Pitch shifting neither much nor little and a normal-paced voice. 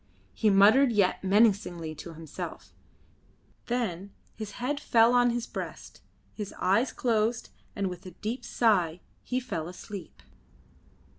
No: average, 4.6 semitones; slow, 130 wpm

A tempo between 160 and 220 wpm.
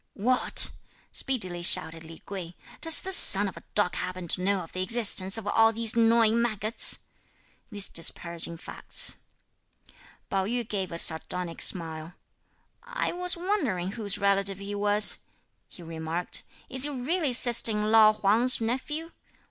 No: average, 150 wpm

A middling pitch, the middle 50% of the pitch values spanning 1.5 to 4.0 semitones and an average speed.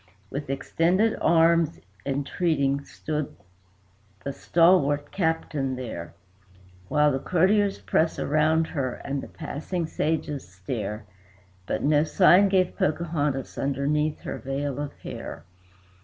No: medium, 150 Hz; average, 3.2 semitones; slow, 110 wpm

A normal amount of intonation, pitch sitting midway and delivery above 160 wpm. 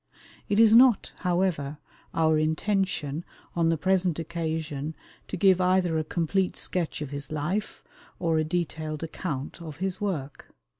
No: average, 3.2 semitones; medium, 165 Hz; average, 145 wpm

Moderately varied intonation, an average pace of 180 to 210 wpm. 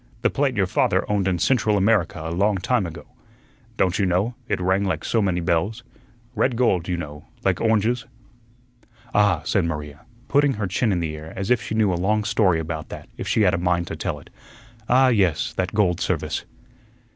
Yes: average, 4.3 semitones; fast, 205 wpm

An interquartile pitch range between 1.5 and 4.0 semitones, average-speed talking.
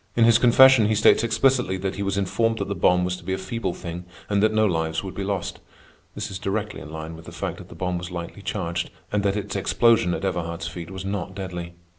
No: average, 3.2 semitones; fast, 250 wpm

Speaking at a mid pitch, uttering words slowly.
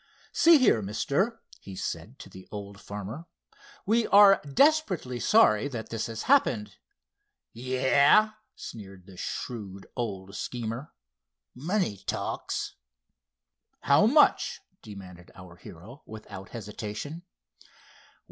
No: low, 110 Hz; slow, 100 wpm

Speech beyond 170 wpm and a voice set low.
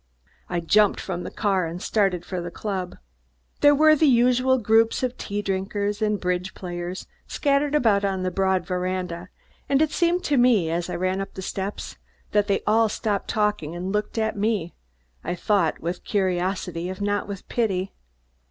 No: average, 180 wpm; high, 200 Hz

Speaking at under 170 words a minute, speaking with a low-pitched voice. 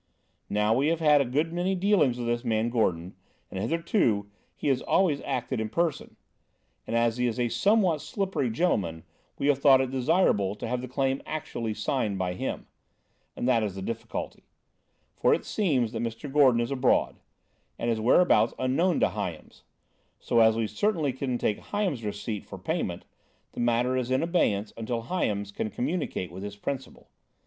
No: average, 180 wpm; low, 125 Hz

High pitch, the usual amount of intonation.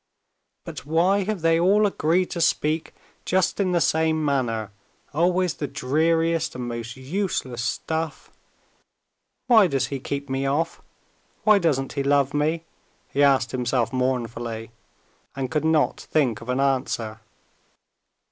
No: medium, 145 Hz; average, 4.4 semitones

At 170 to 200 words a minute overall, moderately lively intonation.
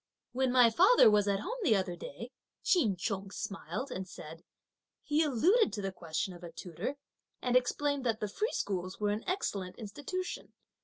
No: average, 175 wpm; wide, 6.8 semitones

